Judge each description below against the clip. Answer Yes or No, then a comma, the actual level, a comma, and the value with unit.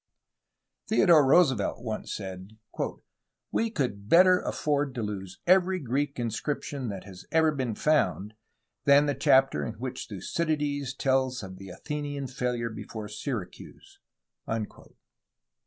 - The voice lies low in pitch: Yes, low, 130 Hz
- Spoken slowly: Yes, slow, 120 wpm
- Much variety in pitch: Yes, wide, 5.7 semitones